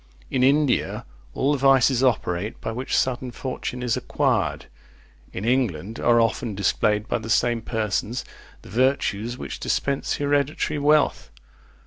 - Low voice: Yes, low, 125 Hz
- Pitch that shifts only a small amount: No, average, 3.2 semitones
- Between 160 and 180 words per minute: No, slow, 135 wpm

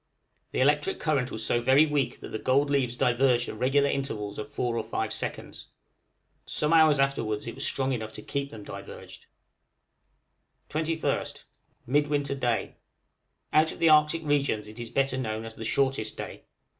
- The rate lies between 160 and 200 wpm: Yes, average, 170 wpm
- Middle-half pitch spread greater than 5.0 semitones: No, average, 3.9 semitones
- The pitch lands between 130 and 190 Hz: Yes, low, 135 Hz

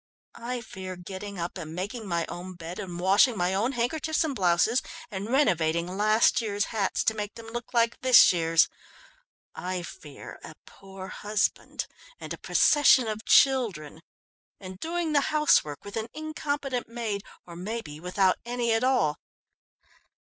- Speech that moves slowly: No, average, 155 wpm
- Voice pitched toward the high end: Yes, high, 205 Hz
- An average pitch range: Yes, average, 5.0 semitones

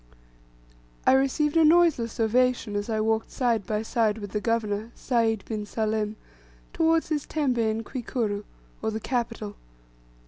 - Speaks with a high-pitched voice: Yes, high, 225 Hz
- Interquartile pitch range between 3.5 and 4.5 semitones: No, average, 2.9 semitones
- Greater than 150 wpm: No, average, 145 wpm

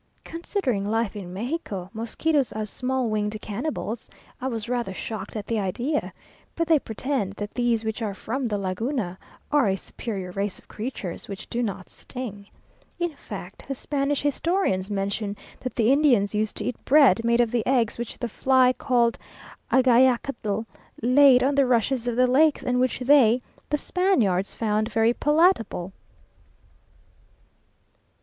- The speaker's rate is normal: Yes, average, 155 wpm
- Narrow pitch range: No, average, 4.1 semitones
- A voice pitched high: Yes, high, 235 Hz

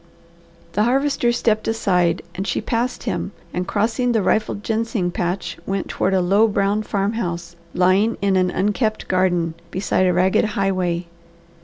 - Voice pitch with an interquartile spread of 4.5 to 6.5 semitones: No, average, 3.4 semitones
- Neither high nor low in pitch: No, high, 195 Hz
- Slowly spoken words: No, average, 150 wpm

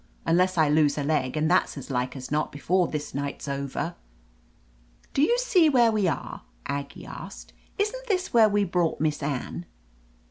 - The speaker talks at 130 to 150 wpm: No, average, 180 wpm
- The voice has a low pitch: No, medium, 160 Hz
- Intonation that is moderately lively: No, wide, 7.1 semitones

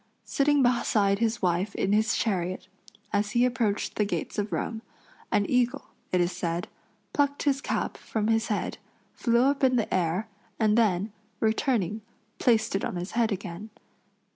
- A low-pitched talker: No, high, 220 Hz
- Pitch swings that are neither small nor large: Yes, average, 3.3 semitones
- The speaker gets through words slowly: No, average, 165 wpm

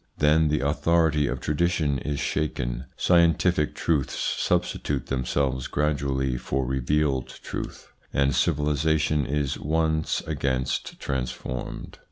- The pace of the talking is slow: Yes, slow, 110 wpm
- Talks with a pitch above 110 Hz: No, very low, 75 Hz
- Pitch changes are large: No, narrow, 2.5 semitones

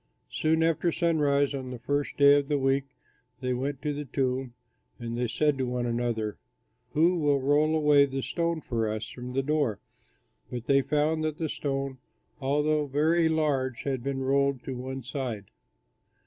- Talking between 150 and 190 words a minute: Yes, average, 175 wpm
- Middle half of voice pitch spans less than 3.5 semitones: Yes, average, 2.8 semitones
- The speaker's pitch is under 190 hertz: Yes, medium, 140 Hz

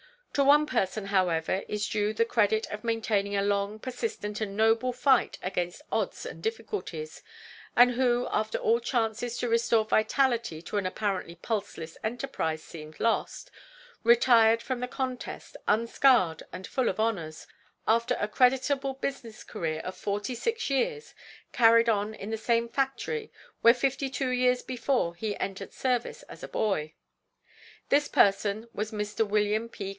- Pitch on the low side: No, high, 225 Hz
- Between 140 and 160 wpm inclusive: Yes, average, 150 wpm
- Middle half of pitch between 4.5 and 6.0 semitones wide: No, average, 3.6 semitones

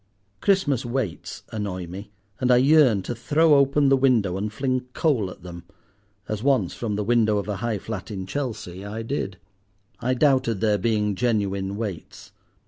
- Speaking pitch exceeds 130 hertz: No, low, 110 Hz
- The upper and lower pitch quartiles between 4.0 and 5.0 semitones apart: Yes, average, 4.4 semitones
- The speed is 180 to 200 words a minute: No, average, 165 wpm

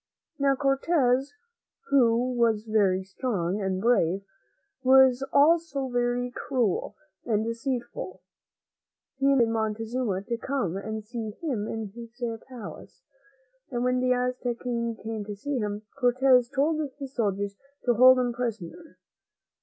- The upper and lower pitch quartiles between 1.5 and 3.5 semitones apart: Yes, average, 3.1 semitones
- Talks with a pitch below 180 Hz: No, high, 240 Hz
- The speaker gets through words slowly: Yes, slow, 130 wpm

